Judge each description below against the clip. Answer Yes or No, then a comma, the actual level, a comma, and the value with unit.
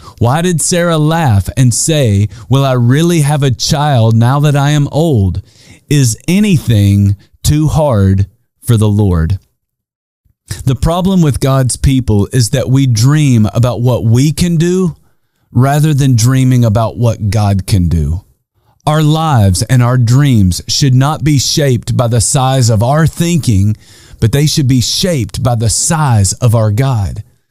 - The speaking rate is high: No, average, 155 wpm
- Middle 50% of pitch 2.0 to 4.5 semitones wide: No, average, 5.0 semitones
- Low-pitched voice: Yes, low, 125 Hz